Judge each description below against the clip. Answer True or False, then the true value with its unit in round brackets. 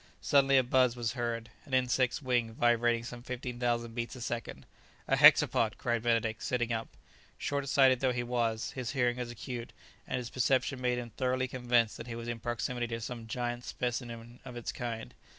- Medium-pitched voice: False (120 Hz)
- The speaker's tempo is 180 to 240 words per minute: True (190 wpm)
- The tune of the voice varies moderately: False (1.3 semitones)